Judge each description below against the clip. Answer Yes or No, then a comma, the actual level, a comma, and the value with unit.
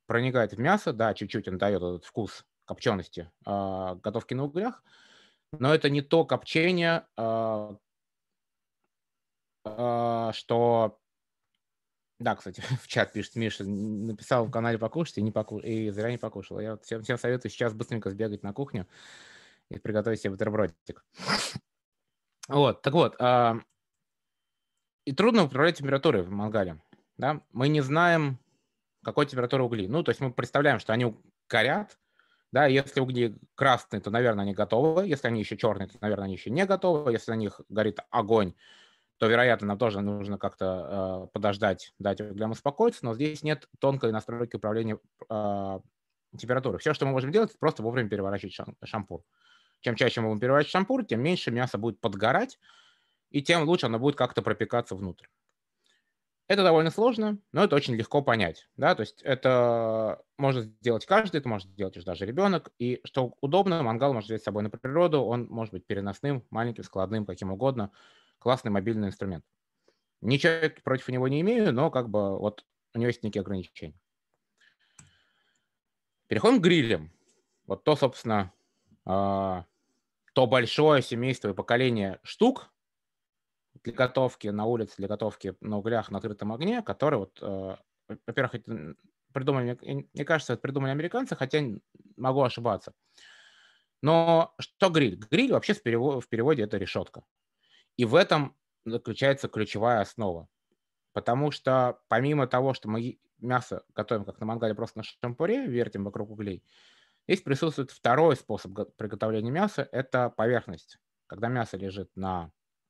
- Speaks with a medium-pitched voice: No, low, 115 Hz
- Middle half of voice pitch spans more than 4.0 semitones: Yes, average, 4.7 semitones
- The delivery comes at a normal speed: Yes, average, 150 wpm